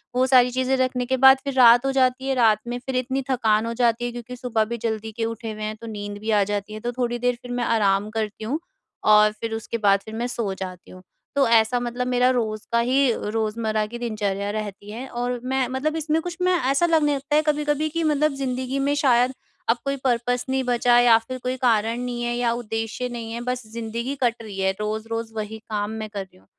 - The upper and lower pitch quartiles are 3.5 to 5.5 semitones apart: No, average, 2.9 semitones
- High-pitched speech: Yes, high, 240 Hz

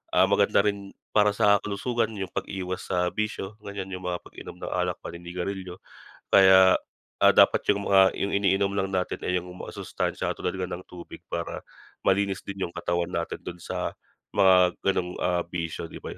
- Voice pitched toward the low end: Yes, very low, 95 Hz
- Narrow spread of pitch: Yes, narrow, 1.9 semitones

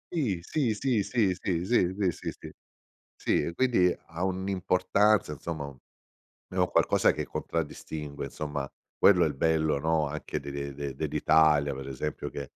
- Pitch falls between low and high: No, very low, 80 Hz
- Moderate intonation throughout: Yes, average, 4.7 semitones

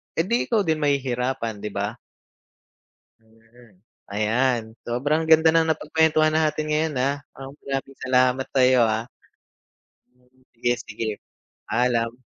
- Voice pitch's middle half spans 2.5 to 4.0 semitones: No, average, 4.6 semitones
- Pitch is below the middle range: Yes, low, 130 Hz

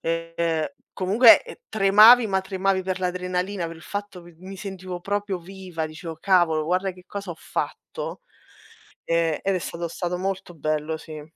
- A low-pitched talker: No, medium, 180 Hz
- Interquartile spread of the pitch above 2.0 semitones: Yes, narrow, 2.6 semitones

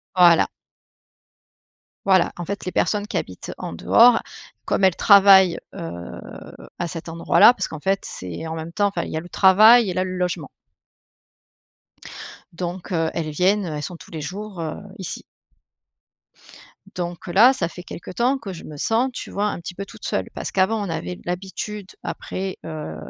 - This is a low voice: No, medium, 180 Hz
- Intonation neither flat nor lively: Yes, average, 3.4 semitones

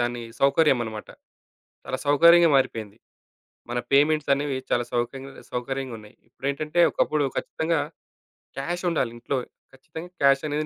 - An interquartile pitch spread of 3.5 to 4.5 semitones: Yes, average, 3.9 semitones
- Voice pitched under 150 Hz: Yes, medium, 140 Hz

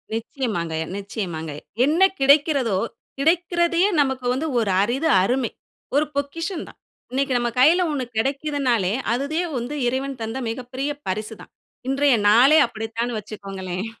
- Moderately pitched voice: No, very high, 255 Hz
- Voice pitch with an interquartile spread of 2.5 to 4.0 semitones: No, average, 4.7 semitones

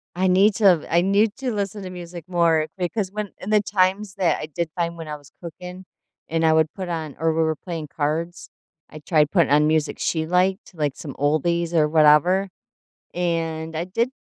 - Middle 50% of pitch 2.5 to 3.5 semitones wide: Yes, average, 2.9 semitones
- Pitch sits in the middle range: Yes, medium, 170 Hz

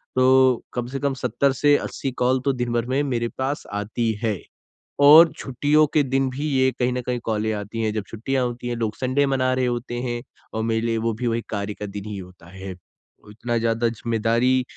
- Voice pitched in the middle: No, low, 120 Hz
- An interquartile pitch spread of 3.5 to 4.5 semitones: No, narrow, 2.5 semitones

